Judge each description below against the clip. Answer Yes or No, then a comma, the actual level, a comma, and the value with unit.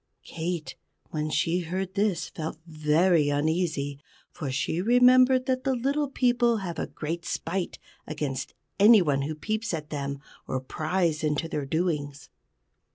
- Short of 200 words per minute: Yes, average, 150 wpm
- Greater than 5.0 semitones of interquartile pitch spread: Yes, wide, 5.5 semitones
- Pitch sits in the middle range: Yes, medium, 165 Hz